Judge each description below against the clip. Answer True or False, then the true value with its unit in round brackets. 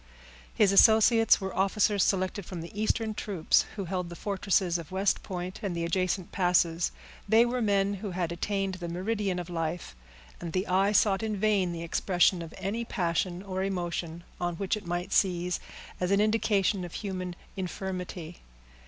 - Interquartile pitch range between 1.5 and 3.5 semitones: True (2.5 semitones)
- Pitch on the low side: False (185 Hz)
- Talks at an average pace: True (170 wpm)